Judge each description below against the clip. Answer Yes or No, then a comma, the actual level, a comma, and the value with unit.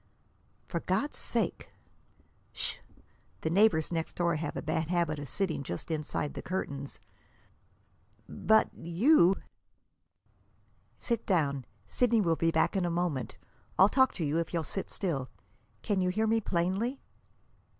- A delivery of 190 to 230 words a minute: No, average, 140 wpm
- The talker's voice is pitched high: No, medium, 170 Hz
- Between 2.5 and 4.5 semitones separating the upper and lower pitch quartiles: Yes, average, 3.9 semitones